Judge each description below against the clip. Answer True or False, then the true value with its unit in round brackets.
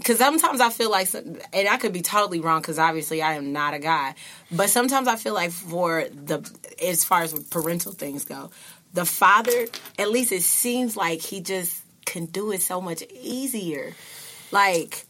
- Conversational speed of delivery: True (185 wpm)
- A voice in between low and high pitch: True (180 Hz)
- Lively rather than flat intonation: True (5.7 semitones)